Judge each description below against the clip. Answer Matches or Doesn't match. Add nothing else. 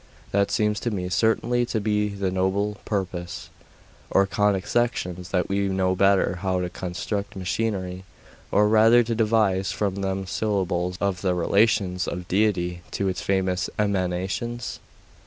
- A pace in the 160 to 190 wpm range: Doesn't match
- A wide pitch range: Doesn't match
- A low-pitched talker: Matches